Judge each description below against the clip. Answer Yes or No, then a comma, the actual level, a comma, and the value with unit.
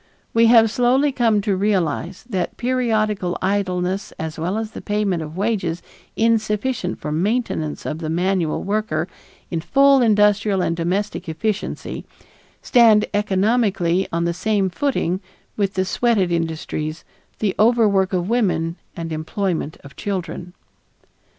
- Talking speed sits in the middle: No, slow, 130 wpm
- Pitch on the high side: Yes, high, 195 Hz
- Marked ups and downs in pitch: No, average, 4.1 semitones